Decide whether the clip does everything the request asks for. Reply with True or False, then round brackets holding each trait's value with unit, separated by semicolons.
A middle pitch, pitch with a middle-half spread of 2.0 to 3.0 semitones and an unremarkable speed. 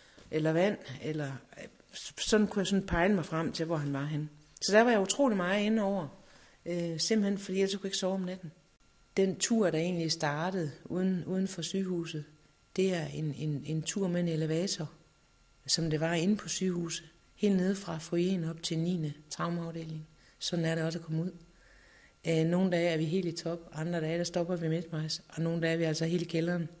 True (170 Hz; 2.7 semitones; 210 wpm)